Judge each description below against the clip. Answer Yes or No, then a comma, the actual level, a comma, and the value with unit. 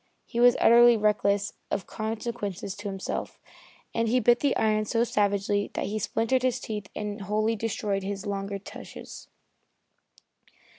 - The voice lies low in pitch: No, high, 210 Hz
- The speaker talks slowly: No, average, 145 wpm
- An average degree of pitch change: No, narrow, 2.2 semitones